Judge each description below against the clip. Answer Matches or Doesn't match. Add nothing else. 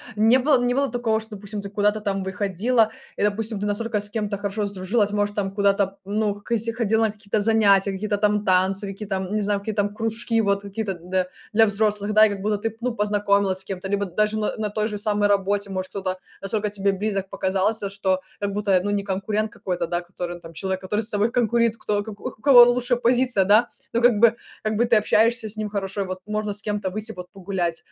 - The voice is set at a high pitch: Matches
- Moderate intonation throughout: Doesn't match